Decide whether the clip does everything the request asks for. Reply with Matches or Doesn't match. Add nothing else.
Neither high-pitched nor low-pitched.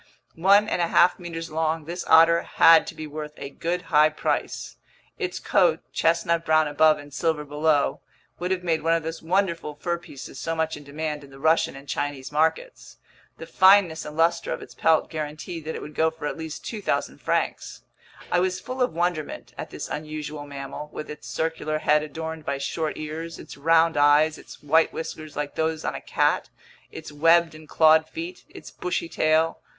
Matches